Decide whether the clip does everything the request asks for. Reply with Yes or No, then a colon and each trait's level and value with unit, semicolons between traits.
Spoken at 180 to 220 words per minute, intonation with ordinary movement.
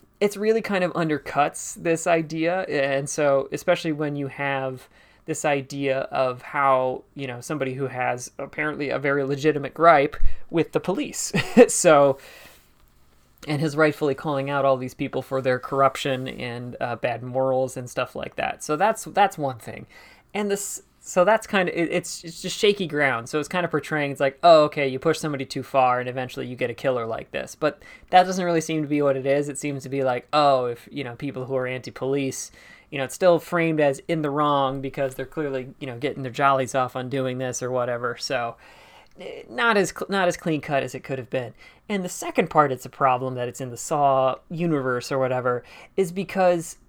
Yes: fast, 205 wpm; average, 3.7 semitones